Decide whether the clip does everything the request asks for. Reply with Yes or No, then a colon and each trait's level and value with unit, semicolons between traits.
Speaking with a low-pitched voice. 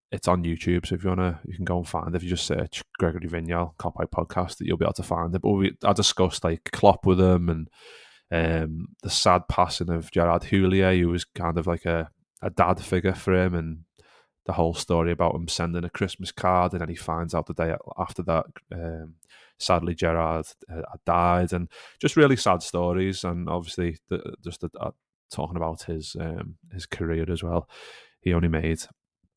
Yes: very low, 85 Hz